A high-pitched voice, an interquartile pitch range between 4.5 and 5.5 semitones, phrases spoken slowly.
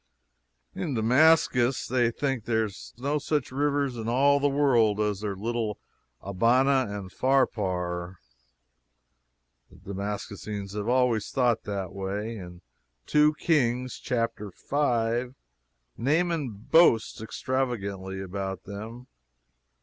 No: low, 115 Hz; average, 4.8 semitones; slow, 110 wpm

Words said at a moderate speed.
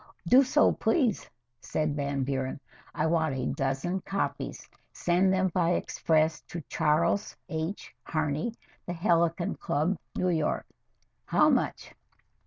No: slow, 125 wpm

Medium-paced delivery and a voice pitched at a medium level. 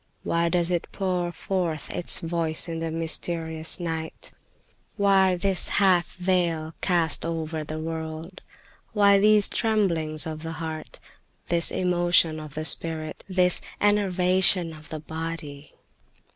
No: slow, 130 wpm; medium, 165 Hz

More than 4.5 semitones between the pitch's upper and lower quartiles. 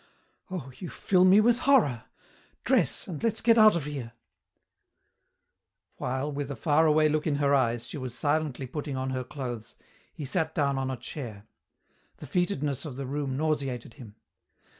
No: average, 3.3 semitones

